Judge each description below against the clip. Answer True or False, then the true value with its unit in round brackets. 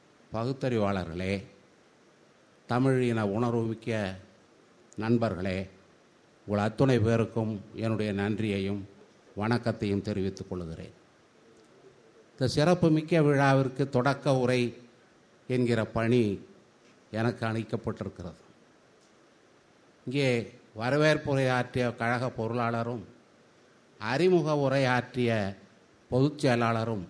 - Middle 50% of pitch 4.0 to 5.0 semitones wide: False (3.4 semitones)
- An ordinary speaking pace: False (70 wpm)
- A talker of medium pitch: False (115 Hz)